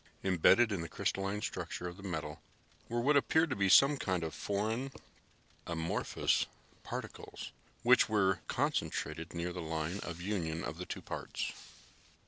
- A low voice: Yes, very low, 95 Hz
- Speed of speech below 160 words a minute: Yes, average, 150 wpm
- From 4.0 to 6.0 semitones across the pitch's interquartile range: Yes, average, 4.7 semitones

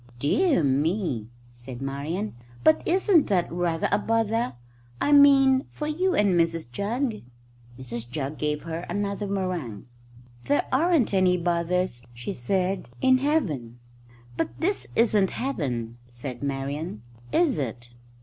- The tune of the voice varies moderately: No, wide, 8.9 semitones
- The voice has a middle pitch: Yes, medium, 175 Hz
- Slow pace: Yes, slow, 130 wpm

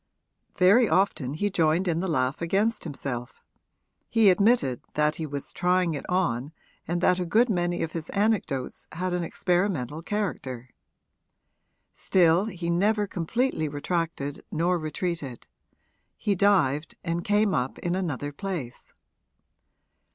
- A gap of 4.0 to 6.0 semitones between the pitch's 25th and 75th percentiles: Yes, average, 4.4 semitones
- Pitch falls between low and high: Yes, medium, 175 Hz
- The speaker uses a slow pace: Yes, slow, 130 wpm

